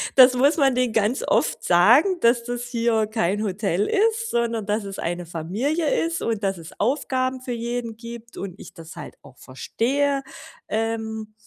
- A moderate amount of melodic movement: Yes, average, 3.9 semitones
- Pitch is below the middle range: No, high, 230 Hz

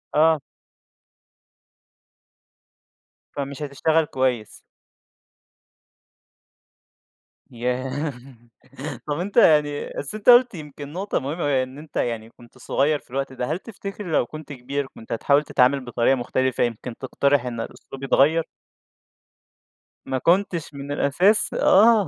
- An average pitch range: Yes, average, 3.6 semitones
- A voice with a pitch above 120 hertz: Yes, medium, 140 Hz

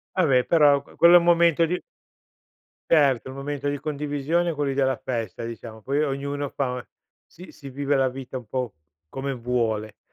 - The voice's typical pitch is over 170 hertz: No, medium, 140 Hz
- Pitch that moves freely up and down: No, average, 2.8 semitones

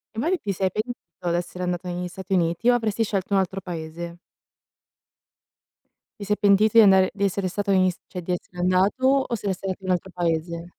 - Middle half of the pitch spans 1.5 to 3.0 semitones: Yes, narrow, 2.5 semitones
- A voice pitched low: No, high, 190 Hz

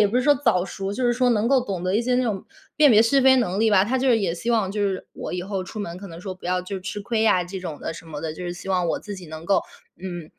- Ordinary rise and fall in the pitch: Yes, average, 4.4 semitones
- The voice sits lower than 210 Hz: Yes, high, 195 Hz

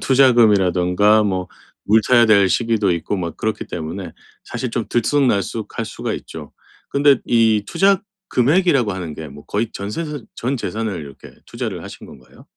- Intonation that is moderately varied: Yes, average, 5.0 semitones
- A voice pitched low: Yes, low, 110 Hz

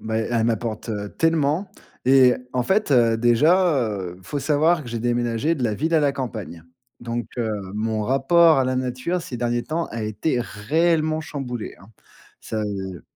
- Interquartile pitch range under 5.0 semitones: No, wide, 5.5 semitones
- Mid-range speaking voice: No, low, 125 Hz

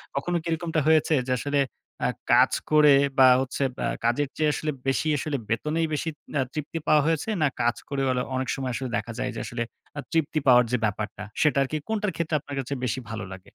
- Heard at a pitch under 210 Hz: Yes, medium, 140 Hz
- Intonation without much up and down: No, average, 3.7 semitones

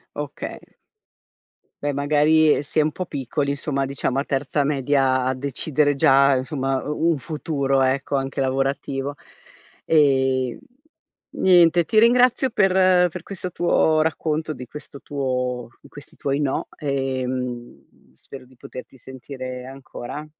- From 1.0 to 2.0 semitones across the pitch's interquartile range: No, narrow, 2.6 semitones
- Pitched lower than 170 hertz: Yes, medium, 140 Hz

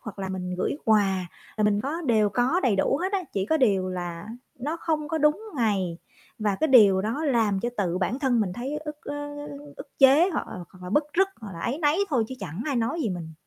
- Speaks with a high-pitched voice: Yes, high, 230 Hz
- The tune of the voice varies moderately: No, wide, 7.2 semitones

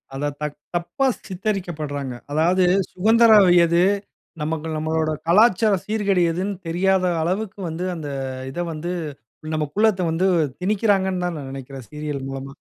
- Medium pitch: Yes, medium, 175 Hz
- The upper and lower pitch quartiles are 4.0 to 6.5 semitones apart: Yes, average, 4.3 semitones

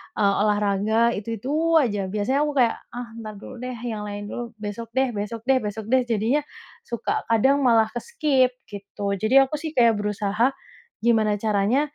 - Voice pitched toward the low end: No, high, 225 Hz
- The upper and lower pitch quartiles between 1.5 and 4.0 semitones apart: Yes, average, 3.7 semitones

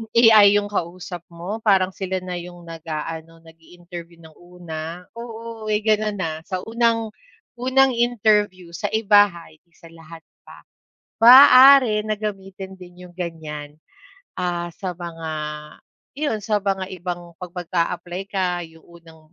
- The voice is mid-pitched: Yes, medium, 180 Hz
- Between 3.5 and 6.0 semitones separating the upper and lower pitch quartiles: Yes, average, 3.8 semitones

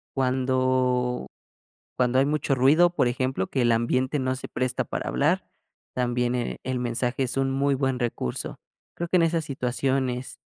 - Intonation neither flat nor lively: No, narrow, 1.4 semitones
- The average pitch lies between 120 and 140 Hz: Yes, low, 130 Hz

